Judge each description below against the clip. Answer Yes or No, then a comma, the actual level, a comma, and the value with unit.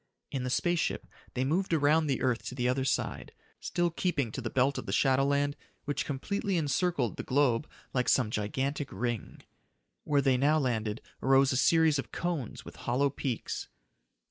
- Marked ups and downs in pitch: No, average, 3.2 semitones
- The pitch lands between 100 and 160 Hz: Yes, low, 135 Hz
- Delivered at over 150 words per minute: Yes, average, 170 wpm